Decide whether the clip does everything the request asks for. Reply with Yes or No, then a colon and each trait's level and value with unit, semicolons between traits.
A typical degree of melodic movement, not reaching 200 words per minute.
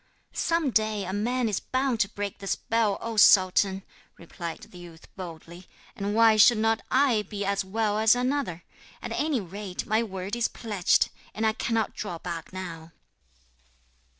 Yes: average, 3.3 semitones; average, 170 wpm